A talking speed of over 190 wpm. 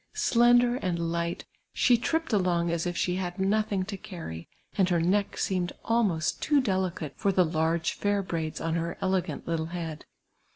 No: average, 170 wpm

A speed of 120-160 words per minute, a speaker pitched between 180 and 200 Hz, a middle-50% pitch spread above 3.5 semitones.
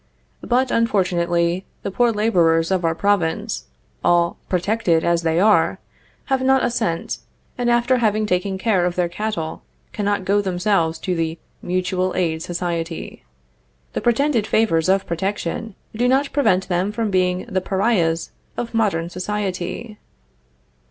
Yes: average, 140 wpm; high, 190 Hz; average, 4.2 semitones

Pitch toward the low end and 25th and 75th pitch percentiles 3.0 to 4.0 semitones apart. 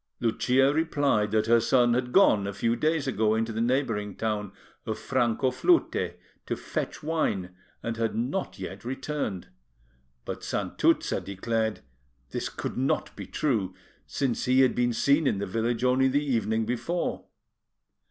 Yes: low, 120 Hz; average, 3.4 semitones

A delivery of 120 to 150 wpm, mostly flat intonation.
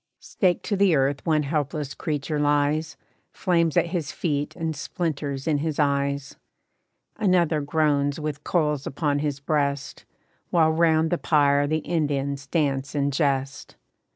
Yes: average, 140 wpm; narrow, 2.2 semitones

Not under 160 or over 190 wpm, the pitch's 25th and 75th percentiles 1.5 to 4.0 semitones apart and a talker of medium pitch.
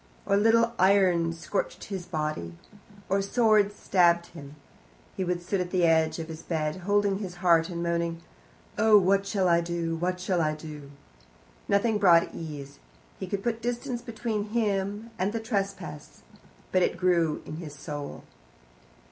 Yes: average, 165 wpm; average, 3.6 semitones; medium, 180 Hz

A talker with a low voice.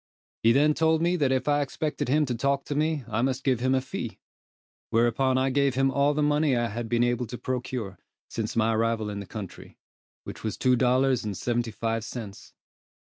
Yes: low, 125 Hz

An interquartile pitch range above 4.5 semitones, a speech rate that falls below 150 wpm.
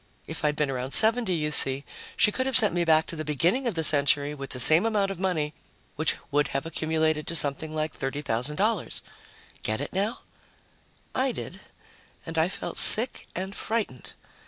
No: average, 5.1 semitones; average, 180 wpm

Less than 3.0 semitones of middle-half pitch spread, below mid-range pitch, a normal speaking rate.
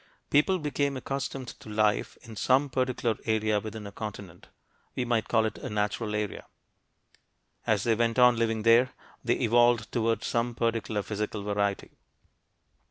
Yes: narrow, 2.4 semitones; low, 115 Hz; average, 150 wpm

